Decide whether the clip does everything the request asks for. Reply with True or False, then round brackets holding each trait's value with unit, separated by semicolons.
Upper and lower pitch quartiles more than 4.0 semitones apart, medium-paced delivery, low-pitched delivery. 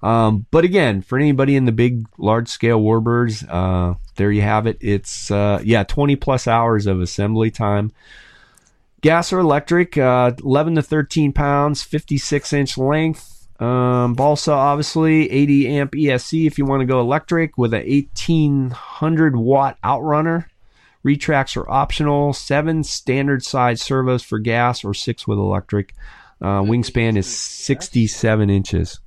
True (4.9 semitones; 145 wpm; 125 Hz)